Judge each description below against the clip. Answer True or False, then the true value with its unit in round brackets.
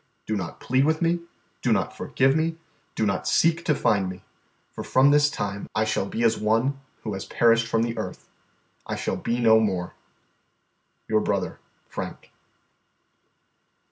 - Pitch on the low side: True (115 Hz)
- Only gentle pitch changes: False (5.0 semitones)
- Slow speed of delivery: False (165 wpm)